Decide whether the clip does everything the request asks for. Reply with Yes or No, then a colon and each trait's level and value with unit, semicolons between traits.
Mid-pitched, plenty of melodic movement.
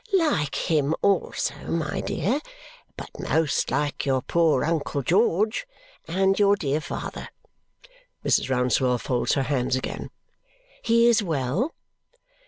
Yes: medium, 160 Hz; wide, 6.6 semitones